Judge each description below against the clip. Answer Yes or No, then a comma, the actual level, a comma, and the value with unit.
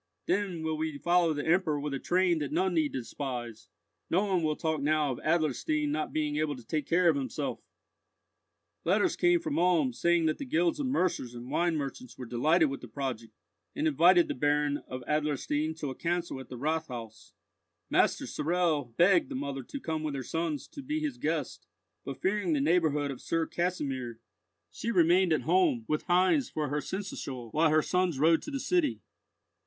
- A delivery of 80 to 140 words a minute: No, average, 190 wpm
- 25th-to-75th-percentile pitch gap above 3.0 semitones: Yes, average, 4.1 semitones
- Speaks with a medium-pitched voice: Yes, medium, 155 Hz